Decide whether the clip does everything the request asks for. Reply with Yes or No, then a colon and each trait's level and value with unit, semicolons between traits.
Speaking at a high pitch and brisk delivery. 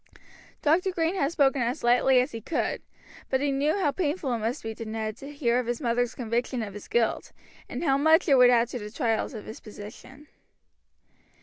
Yes: very high, 250 Hz; fast, 210 wpm